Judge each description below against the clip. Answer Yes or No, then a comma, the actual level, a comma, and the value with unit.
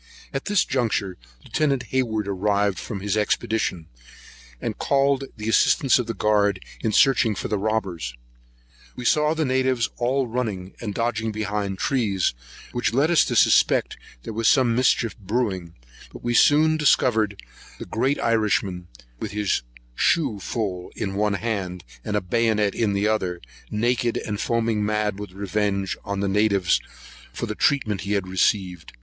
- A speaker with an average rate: Yes, average, 160 wpm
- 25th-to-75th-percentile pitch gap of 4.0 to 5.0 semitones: No, average, 3.4 semitones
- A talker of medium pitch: No, low, 105 Hz